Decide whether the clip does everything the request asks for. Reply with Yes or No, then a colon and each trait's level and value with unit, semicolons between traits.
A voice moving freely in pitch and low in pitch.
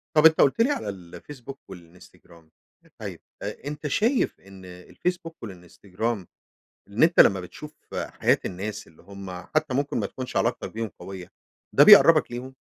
Yes: wide, 8.2 semitones; low, 110 Hz